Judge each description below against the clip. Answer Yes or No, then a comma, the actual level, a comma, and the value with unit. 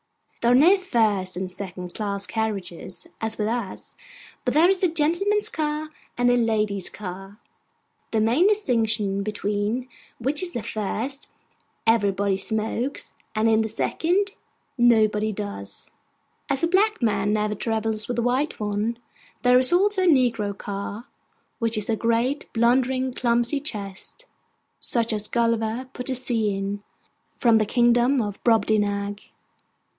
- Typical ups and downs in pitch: Yes, average, 3.8 semitones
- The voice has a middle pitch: No, high, 225 Hz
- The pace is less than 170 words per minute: Yes, average, 150 wpm